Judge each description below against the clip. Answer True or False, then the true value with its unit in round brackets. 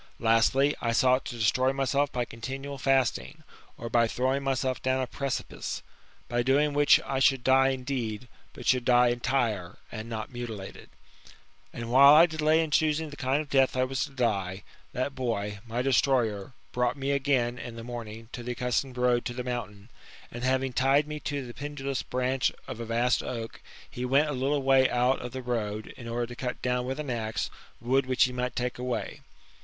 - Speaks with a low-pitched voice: True (125 Hz)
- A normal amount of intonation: False (2.2 semitones)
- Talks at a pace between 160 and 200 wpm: True (195 wpm)